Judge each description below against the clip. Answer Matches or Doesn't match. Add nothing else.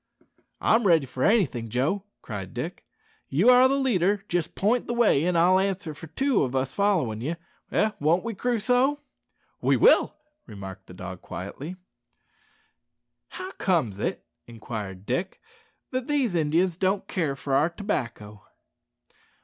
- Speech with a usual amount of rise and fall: Doesn't match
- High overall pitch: Doesn't match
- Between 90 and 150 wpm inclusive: Matches